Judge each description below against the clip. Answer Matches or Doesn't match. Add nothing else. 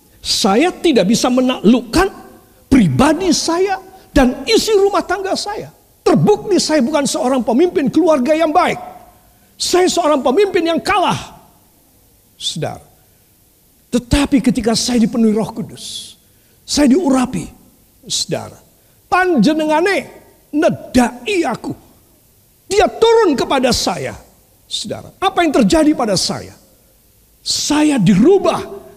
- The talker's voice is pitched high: Matches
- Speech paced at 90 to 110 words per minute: Matches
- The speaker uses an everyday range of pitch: Doesn't match